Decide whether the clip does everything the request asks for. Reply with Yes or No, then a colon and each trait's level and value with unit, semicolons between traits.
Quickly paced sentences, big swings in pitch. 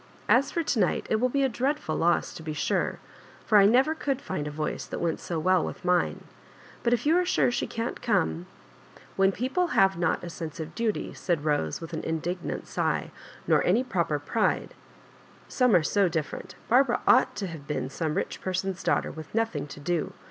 Yes: fast, 220 wpm; wide, 7.1 semitones